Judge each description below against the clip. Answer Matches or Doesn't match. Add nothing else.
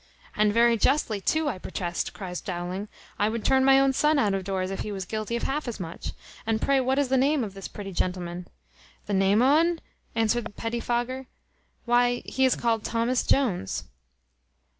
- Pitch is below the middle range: Doesn't match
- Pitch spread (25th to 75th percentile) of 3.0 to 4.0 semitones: Doesn't match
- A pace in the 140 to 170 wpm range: Doesn't match